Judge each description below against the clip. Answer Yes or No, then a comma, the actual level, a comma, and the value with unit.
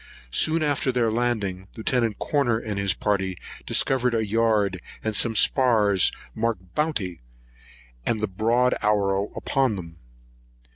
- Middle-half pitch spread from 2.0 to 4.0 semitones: Yes, average, 3.7 semitones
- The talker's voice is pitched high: No, low, 110 Hz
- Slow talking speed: Yes, slow, 130 wpm